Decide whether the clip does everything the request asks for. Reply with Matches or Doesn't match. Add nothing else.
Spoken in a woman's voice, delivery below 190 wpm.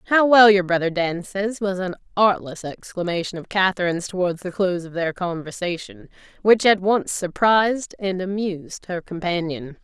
Matches